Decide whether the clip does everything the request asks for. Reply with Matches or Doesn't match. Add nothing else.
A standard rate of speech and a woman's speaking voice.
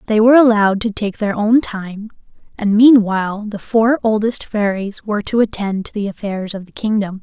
Matches